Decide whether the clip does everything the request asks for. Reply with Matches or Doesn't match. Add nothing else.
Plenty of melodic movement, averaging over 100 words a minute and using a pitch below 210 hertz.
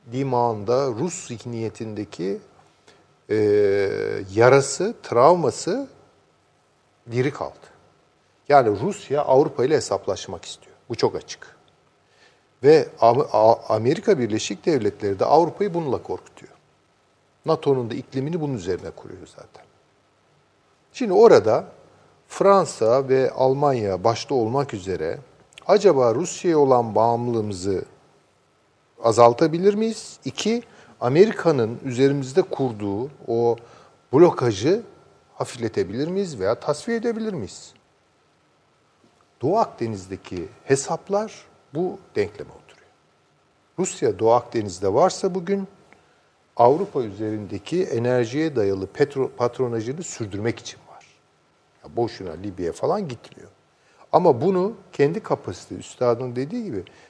Doesn't match